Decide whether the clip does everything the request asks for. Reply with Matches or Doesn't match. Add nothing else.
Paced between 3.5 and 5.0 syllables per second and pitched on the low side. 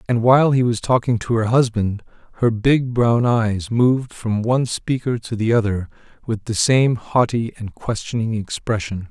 Matches